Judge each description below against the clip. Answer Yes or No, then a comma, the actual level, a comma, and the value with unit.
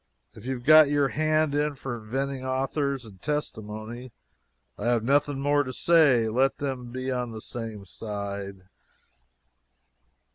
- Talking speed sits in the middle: Yes, average, 145 wpm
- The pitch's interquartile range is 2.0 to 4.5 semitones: Yes, average, 4.2 semitones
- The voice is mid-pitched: No, low, 130 Hz